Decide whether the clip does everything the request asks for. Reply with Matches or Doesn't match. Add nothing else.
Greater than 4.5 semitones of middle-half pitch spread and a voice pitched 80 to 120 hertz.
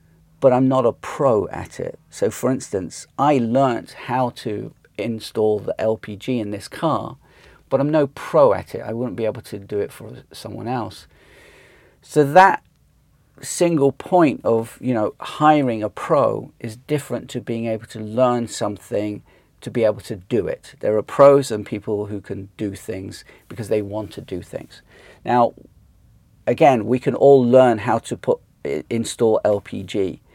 Doesn't match